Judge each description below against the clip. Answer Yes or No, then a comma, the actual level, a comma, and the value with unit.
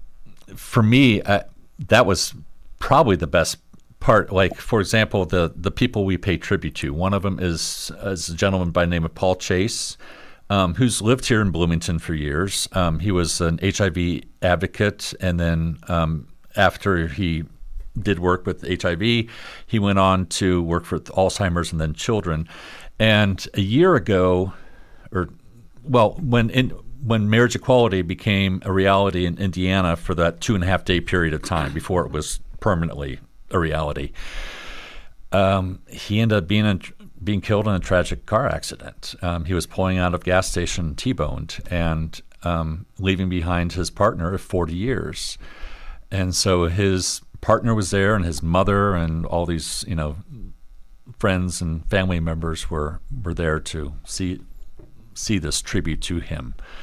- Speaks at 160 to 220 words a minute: Yes, average, 165 wpm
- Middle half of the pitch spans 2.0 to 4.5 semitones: Yes, average, 3.3 semitones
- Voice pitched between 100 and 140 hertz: No, very low, 90 Hz